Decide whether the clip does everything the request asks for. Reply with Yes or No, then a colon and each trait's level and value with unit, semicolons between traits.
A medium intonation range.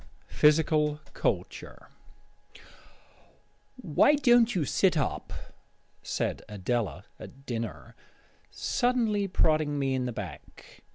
No: wide, 8.1 semitones